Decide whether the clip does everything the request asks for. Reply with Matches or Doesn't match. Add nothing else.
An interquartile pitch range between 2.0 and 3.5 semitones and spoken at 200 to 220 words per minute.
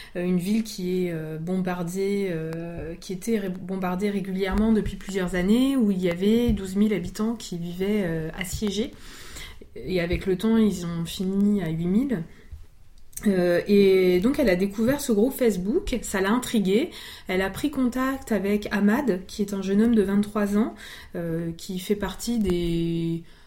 Doesn't match